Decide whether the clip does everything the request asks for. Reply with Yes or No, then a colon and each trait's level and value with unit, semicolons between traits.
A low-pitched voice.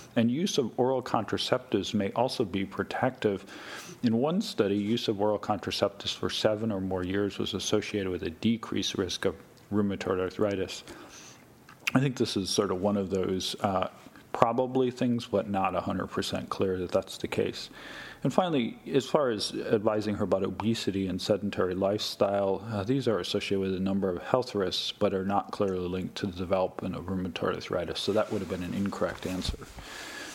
Yes: low, 100 Hz